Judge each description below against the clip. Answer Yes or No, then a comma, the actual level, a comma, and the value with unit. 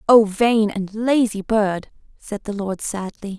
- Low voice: No, high, 210 Hz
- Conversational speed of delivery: Yes, average, 160 wpm